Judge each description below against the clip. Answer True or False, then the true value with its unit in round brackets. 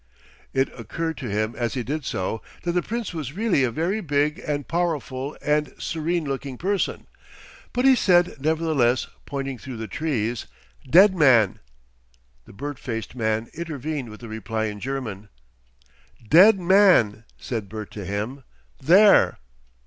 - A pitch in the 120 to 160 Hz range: True (140 Hz)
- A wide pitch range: True (6.6 semitones)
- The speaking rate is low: False (150 wpm)